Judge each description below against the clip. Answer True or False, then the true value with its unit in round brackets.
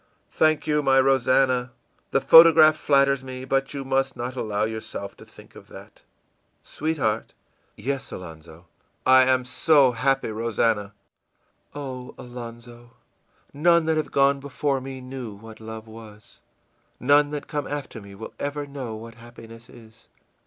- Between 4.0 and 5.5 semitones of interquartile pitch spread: False (3.5 semitones)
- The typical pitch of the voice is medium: False (130 Hz)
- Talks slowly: False (145 wpm)